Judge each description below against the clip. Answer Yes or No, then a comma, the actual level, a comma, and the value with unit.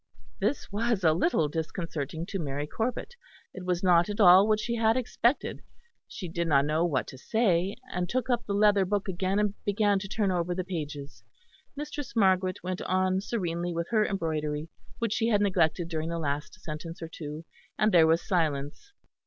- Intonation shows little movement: No, average, 4.1 semitones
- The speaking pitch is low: No, medium, 185 Hz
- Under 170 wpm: No, average, 185 wpm